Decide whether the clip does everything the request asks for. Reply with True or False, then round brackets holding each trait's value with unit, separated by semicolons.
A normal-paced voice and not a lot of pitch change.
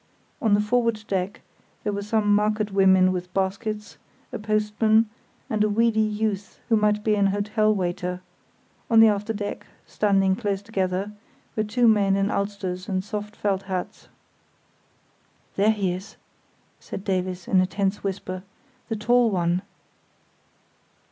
True (145 wpm; 2.0 semitones)